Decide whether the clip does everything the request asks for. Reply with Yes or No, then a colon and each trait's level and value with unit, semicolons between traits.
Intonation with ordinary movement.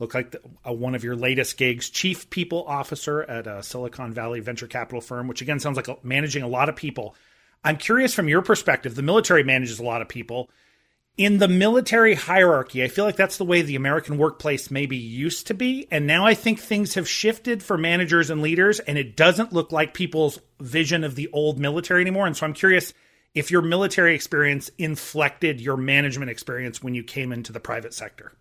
No: wide, 5.8 semitones